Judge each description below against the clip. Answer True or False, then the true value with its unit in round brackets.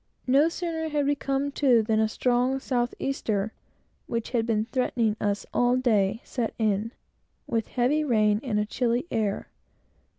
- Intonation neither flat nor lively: True (3.6 semitones)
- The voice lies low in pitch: False (240 Hz)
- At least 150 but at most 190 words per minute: True (160 wpm)